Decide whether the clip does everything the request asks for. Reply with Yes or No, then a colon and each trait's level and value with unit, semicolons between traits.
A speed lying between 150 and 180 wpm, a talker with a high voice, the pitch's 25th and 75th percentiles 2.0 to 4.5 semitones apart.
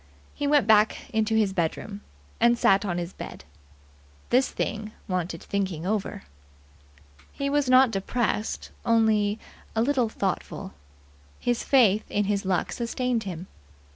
No: slow, 135 wpm; high, 215 Hz; average, 3.6 semitones